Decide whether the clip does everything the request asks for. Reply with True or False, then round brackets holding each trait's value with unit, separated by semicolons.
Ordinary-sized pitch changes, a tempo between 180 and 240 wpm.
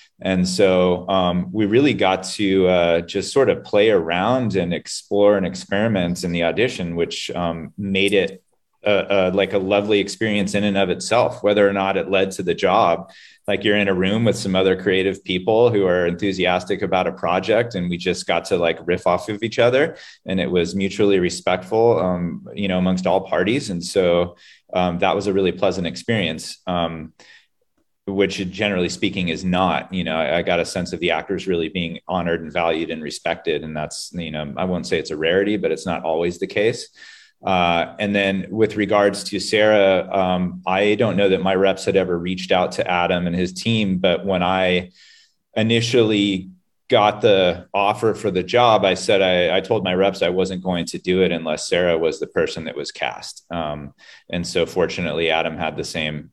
False (2.1 semitones; 200 wpm)